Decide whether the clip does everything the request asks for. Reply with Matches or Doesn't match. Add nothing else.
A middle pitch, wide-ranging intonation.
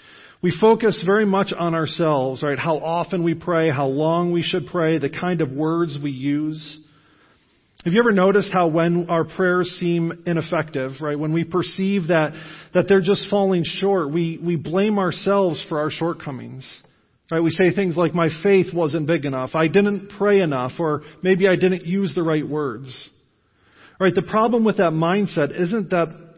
Doesn't match